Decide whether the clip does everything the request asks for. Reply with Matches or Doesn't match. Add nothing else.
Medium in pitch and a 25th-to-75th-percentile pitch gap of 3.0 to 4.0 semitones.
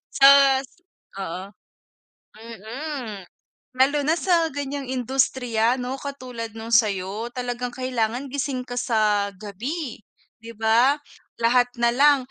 Doesn't match